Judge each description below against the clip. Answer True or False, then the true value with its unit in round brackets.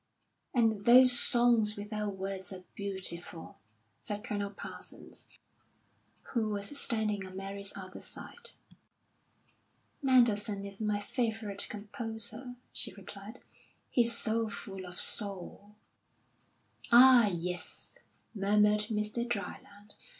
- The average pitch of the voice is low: False (210 Hz)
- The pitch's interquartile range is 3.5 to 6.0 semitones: False (2.5 semitones)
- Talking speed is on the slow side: True (100 wpm)